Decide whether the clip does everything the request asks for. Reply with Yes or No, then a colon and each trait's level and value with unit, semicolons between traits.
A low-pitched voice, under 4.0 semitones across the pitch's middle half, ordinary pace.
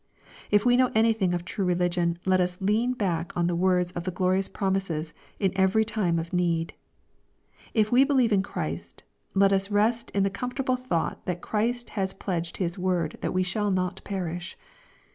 No: high, 190 Hz; average, 3.2 semitones; average, 185 wpm